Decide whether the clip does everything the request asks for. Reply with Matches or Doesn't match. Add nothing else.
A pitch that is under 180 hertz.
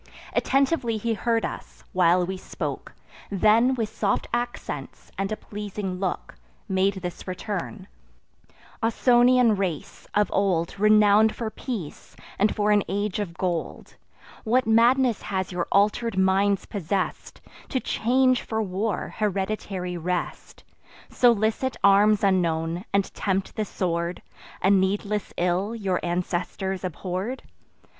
Doesn't match